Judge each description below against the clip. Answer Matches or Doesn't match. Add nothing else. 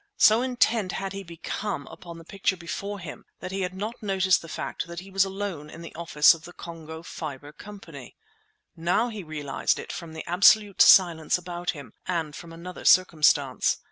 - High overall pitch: Doesn't match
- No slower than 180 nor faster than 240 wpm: Matches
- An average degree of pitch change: Matches